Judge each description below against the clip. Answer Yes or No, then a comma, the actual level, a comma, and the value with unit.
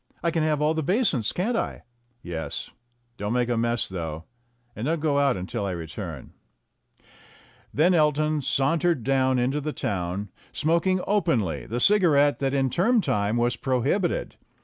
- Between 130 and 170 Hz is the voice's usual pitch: Yes, low, 135 Hz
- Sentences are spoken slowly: No, average, 155 wpm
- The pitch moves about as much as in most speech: No, wide, 6.8 semitones